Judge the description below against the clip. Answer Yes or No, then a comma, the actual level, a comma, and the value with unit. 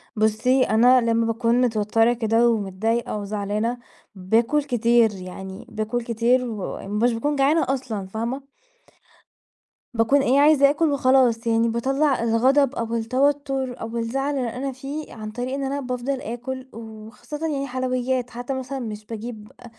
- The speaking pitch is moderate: No, high, 240 Hz